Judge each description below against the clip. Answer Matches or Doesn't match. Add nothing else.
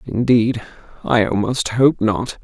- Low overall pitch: Matches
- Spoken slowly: Matches